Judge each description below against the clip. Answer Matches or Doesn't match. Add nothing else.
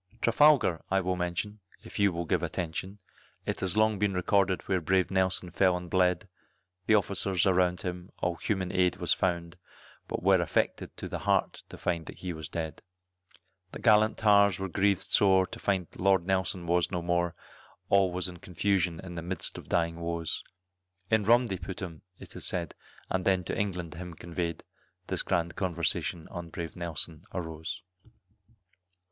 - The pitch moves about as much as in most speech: Doesn't match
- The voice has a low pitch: Matches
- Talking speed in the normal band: Matches